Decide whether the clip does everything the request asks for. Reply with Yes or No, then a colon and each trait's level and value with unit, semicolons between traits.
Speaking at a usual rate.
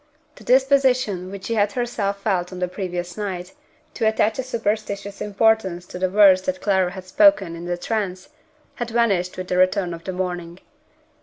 Yes: average, 180 wpm